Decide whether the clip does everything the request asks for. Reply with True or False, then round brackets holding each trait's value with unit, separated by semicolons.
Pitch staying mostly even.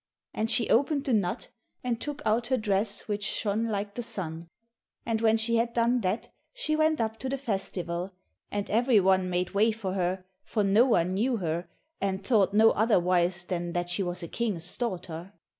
False (4.1 semitones)